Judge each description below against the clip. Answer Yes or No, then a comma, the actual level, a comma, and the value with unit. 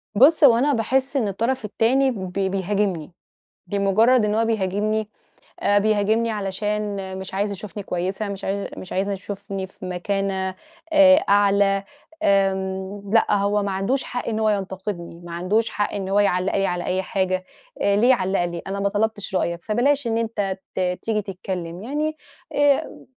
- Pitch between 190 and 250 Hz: Yes, high, 200 Hz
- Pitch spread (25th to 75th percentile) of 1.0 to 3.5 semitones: Yes, narrow, 2.6 semitones